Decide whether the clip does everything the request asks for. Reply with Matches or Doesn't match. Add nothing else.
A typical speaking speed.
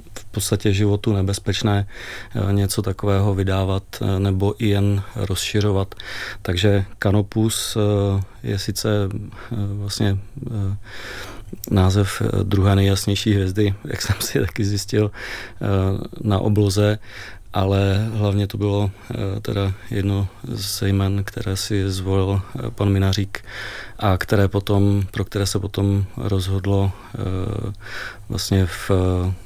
Doesn't match